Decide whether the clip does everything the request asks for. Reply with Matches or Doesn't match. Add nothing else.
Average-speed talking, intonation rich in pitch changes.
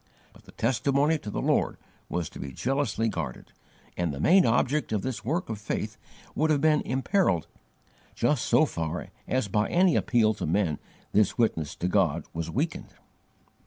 Matches